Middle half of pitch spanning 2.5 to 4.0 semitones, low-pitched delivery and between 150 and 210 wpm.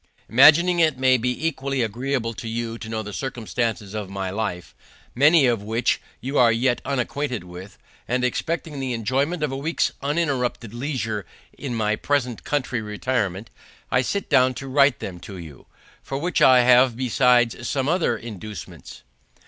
Yes: average, 3.6 semitones; low, 125 Hz; average, 165 wpm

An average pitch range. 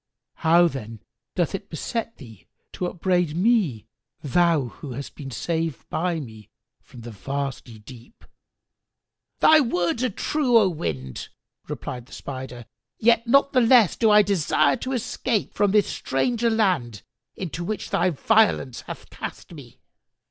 No: wide, 8.7 semitones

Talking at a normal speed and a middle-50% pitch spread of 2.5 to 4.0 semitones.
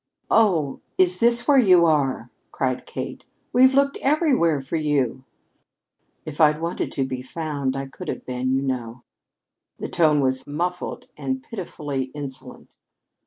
No: average, 145 wpm; average, 5.3 semitones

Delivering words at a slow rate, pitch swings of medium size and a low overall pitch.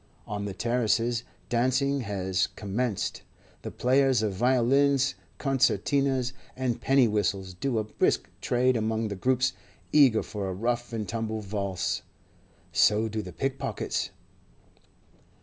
Yes: slow, 125 wpm; average, 3.8 semitones; low, 115 Hz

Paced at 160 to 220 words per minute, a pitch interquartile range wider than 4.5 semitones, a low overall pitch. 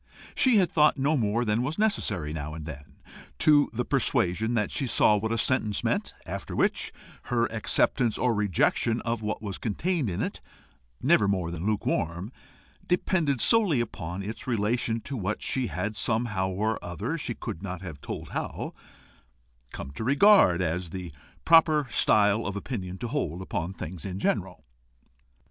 Yes: average, 165 wpm; average, 5.3 semitones; low, 110 Hz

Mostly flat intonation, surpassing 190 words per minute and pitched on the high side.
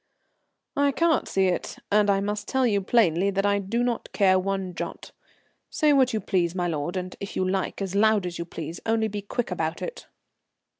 No: average, 3.2 semitones; fast, 205 wpm; high, 200 Hz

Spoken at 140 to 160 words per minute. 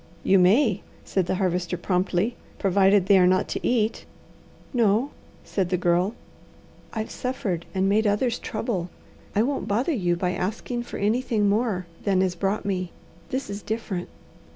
Yes: average, 155 wpm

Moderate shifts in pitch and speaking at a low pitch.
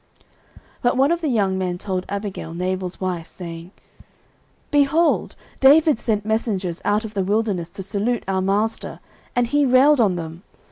No: average, 4.9 semitones; high, 205 Hz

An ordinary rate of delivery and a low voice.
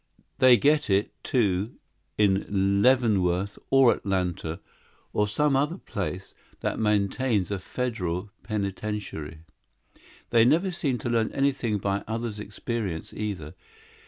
No: slow, 115 wpm; low, 105 Hz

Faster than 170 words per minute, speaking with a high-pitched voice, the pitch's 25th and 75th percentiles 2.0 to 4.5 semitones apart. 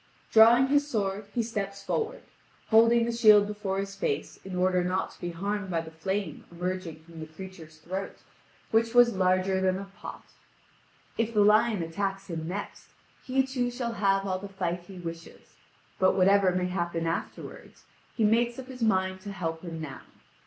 Yes: average, 180 wpm; high, 195 Hz; average, 3.5 semitones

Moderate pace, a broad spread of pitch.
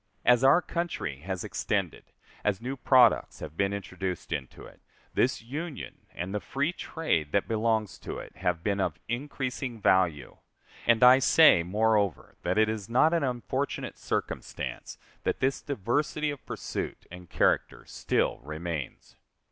Yes: average, 150 wpm; wide, 6.5 semitones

